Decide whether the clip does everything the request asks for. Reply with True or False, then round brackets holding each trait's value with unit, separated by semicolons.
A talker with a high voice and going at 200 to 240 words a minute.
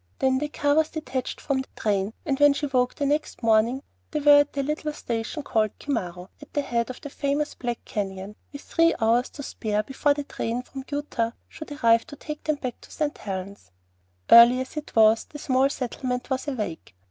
True (260 Hz; 205 wpm)